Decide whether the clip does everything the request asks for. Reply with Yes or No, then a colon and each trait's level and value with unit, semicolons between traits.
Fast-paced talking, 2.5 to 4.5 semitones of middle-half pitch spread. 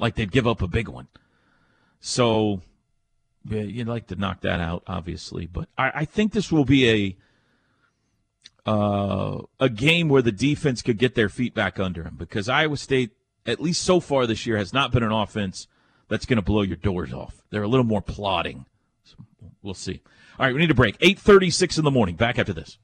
No: fast, 210 wpm; average, 4.9 semitones